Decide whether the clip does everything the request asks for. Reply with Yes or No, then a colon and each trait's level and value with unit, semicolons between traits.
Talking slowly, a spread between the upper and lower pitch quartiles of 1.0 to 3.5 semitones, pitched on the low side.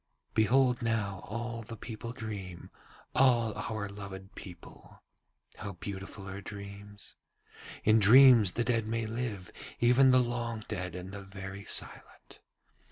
Yes: slow, 130 wpm; average, 3.0 semitones; low, 110 Hz